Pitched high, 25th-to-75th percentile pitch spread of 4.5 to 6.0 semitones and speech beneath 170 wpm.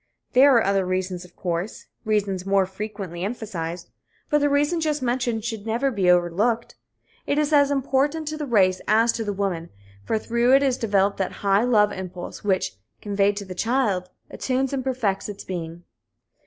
No: high, 210 Hz; average, 5.2 semitones; average, 180 wpm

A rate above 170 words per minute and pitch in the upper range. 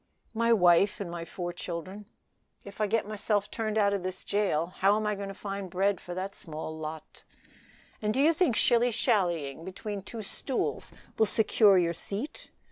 Yes: average, 180 wpm; high, 200 Hz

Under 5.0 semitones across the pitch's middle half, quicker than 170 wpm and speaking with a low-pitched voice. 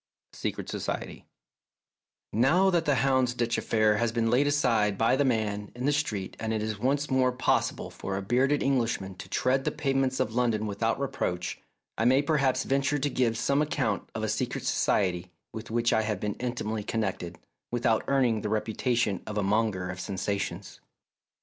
Yes: average, 4.0 semitones; average, 180 wpm; low, 115 Hz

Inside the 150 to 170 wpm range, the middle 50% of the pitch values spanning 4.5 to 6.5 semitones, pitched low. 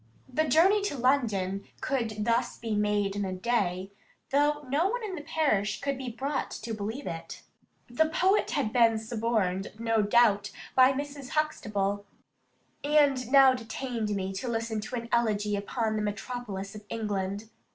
No: average, 160 wpm; average, 4.9 semitones; high, 230 Hz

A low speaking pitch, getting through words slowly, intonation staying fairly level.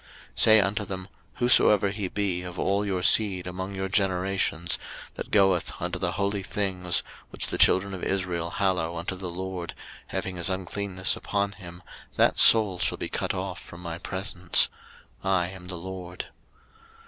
No: very low, 95 Hz; average, 165 wpm; narrow, 1.7 semitones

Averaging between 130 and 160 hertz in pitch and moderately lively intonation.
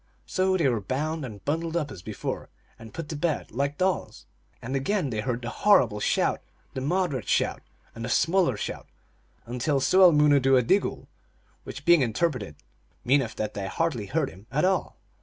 No: medium, 140 Hz; wide, 6.2 semitones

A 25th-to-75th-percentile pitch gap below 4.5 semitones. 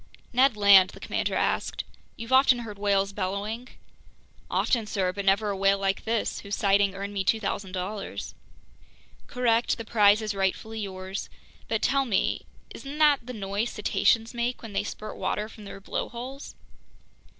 Yes: average, 2.9 semitones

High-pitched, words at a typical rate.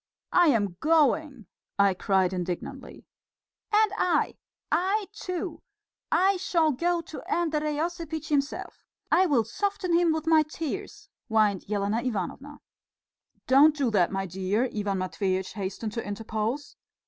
No: very high, 280 Hz; slow, 130 wpm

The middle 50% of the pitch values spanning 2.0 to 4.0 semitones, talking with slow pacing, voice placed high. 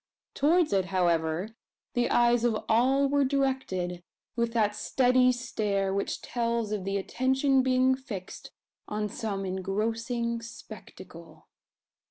No: average, 4.5 semitones; slow, 120 wpm; high, 230 Hz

